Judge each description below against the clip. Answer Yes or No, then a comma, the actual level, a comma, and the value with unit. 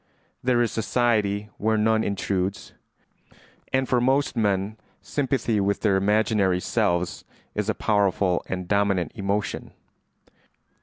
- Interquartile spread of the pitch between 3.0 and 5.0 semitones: No, narrow, 2.4 semitones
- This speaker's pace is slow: Yes, slow, 115 wpm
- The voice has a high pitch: No, low, 105 Hz